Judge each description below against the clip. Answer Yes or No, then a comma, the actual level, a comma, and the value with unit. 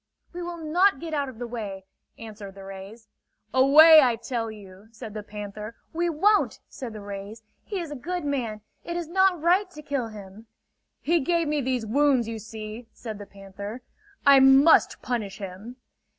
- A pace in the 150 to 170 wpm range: No, average, 180 wpm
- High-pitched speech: Yes, high, 240 Hz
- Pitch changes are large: Yes, wide, 6.3 semitones